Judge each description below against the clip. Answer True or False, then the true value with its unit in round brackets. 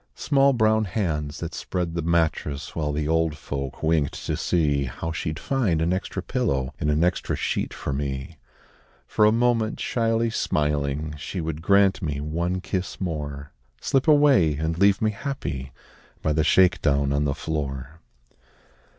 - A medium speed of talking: True (160 wpm)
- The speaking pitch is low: True (80 Hz)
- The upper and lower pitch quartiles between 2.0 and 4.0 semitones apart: False (5.1 semitones)